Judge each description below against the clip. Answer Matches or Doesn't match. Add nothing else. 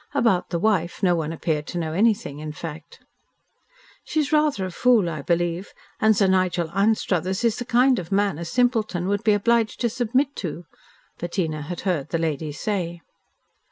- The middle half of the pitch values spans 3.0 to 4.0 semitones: Doesn't match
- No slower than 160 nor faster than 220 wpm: Matches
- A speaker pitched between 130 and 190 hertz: Matches